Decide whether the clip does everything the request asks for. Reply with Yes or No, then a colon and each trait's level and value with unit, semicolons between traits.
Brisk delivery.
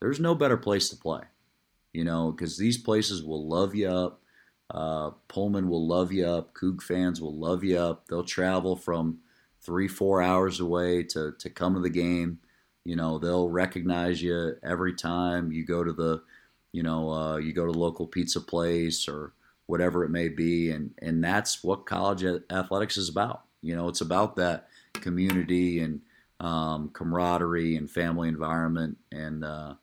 No: average, 175 wpm